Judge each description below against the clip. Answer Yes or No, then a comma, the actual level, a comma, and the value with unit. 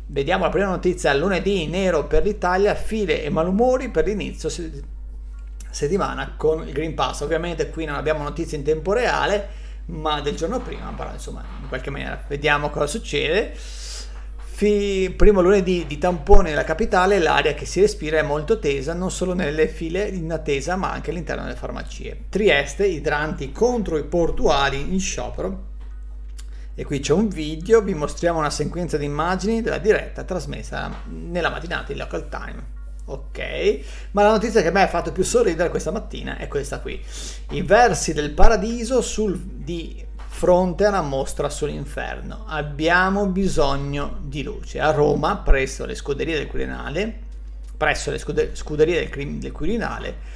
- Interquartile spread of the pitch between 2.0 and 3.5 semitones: No, wide, 5.6 semitones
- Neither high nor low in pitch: Yes, medium, 165 Hz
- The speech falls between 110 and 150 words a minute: No, average, 160 wpm